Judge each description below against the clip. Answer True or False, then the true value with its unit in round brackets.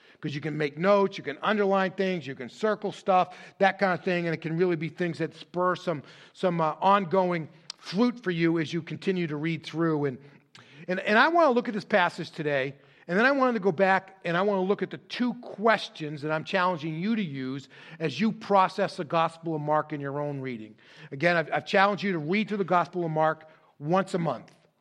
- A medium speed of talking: False (235 wpm)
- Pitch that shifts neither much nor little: True (3.8 semitones)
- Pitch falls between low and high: True (175 Hz)